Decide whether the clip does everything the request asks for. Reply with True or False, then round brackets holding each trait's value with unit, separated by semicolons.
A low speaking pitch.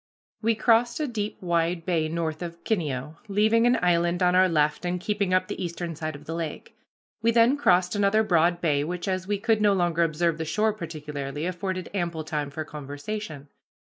False (175 Hz)